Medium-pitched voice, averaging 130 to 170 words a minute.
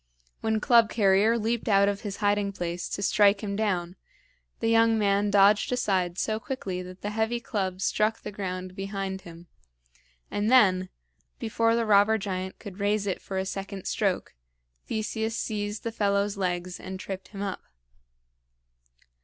No: high, 200 Hz; average, 160 wpm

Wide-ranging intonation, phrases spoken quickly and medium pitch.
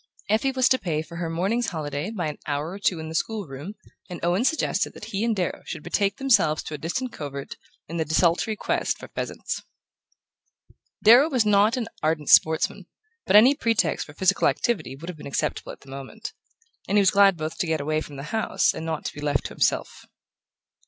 Yes: wide, 5.8 semitones; fast, 215 wpm; medium, 175 Hz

